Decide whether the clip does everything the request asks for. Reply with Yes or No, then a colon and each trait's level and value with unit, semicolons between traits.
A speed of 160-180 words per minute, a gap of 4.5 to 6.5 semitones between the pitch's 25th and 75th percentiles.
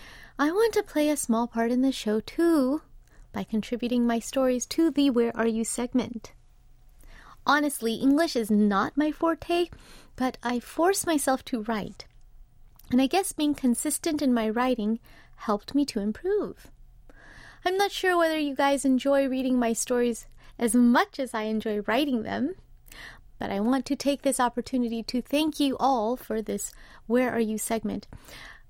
No: average, 165 wpm; average, 4.0 semitones